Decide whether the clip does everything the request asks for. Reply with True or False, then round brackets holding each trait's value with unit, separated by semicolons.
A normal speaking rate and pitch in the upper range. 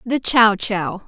True (165 wpm; 220 Hz)